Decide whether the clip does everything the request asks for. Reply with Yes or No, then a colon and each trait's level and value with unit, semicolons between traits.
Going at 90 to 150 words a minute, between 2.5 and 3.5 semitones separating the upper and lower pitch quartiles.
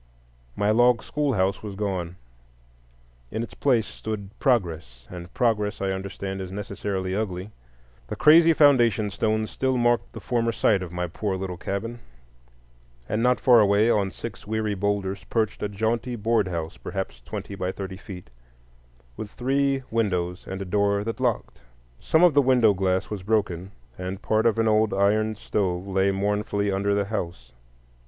No: average, 160 wpm; average, 3.1 semitones